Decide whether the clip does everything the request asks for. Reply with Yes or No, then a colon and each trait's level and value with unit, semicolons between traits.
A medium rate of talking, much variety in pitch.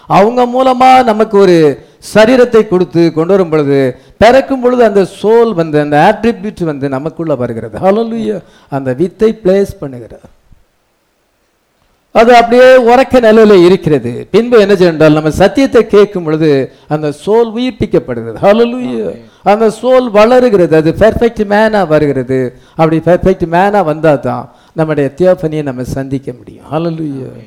No: slow, 125 wpm; wide, 6.7 semitones